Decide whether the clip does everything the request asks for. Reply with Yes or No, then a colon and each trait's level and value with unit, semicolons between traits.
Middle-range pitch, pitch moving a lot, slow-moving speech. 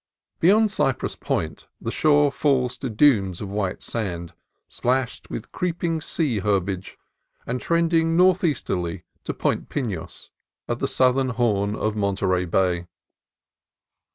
No: low, 120 Hz; wide, 7.3 semitones; slow, 125 wpm